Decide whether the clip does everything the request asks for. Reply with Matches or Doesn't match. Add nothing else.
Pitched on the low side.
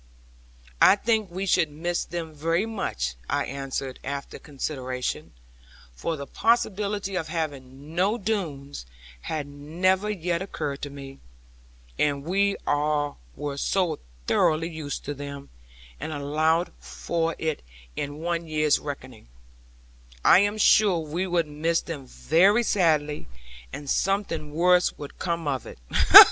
Doesn't match